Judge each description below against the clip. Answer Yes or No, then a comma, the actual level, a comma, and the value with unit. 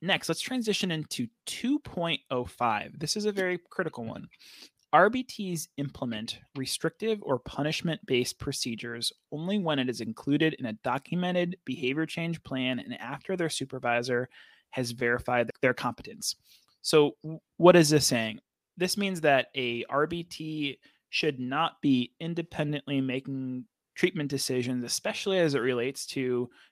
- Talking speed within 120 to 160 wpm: Yes, slow, 135 wpm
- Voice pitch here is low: No, medium, 145 Hz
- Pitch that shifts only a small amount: No, average, 5.3 semitones